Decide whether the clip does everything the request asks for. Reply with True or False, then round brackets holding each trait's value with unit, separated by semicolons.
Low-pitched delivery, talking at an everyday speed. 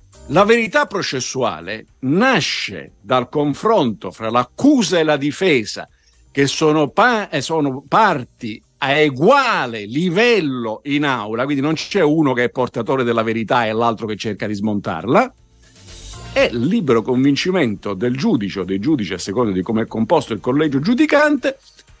True (130 Hz; 145 wpm)